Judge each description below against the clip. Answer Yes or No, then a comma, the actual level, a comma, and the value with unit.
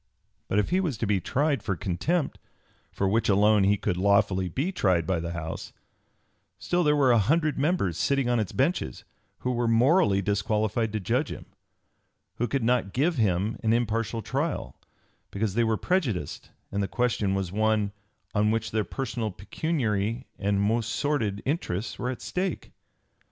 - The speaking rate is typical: Yes, average, 170 wpm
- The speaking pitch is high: No, low, 110 Hz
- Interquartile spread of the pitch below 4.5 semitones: No, average, 5.0 semitones